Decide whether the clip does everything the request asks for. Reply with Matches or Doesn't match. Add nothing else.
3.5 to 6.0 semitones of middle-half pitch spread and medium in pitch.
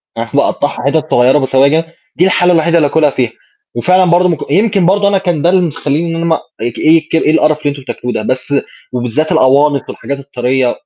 Matches